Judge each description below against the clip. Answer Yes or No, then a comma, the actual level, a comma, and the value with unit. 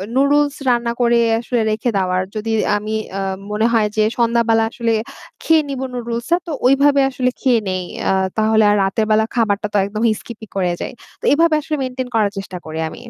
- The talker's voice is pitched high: Yes, high, 230 Hz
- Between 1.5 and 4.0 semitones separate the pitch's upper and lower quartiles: Yes, average, 3.4 semitones